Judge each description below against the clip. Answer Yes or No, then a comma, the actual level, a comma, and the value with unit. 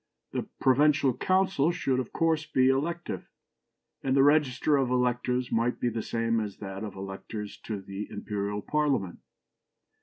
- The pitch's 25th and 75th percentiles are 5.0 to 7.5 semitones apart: Yes, wide, 5.4 semitones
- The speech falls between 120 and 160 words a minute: Yes, average, 150 wpm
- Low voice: Yes, low, 125 Hz